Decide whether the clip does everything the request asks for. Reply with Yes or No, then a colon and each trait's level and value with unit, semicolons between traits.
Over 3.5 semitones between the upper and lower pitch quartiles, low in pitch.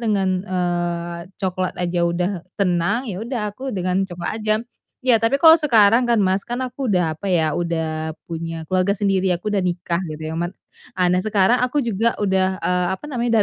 No: average, 4.3 semitones; high, 190 Hz